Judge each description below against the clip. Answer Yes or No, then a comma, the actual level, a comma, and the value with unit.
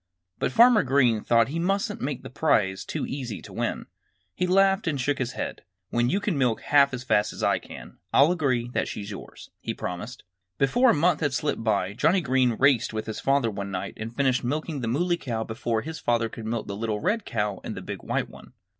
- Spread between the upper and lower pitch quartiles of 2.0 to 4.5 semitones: No, wide, 5.5 semitones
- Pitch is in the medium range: No, low, 130 Hz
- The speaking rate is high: Yes, fast, 225 wpm